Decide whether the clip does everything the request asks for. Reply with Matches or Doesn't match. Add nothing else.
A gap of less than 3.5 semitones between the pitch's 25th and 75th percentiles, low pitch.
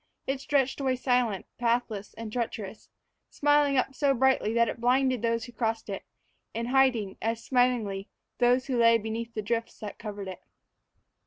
Doesn't match